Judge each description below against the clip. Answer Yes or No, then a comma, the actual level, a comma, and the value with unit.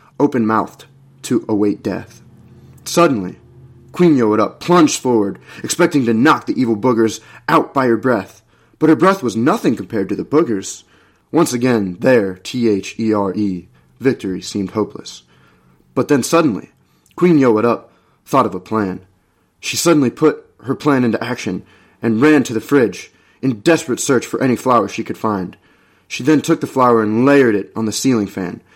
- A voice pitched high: No, low, 115 Hz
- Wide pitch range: No, average, 5.0 semitones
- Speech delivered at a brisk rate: No, average, 175 wpm